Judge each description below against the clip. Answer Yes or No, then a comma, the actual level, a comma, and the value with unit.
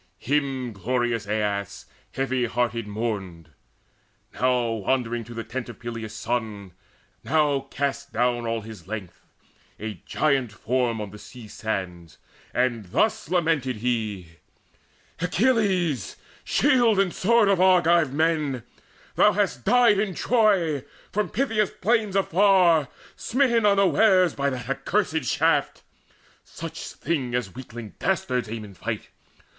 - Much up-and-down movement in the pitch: Yes, wide, 8.2 semitones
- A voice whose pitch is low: Yes, low, 130 Hz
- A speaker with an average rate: No, slow, 125 wpm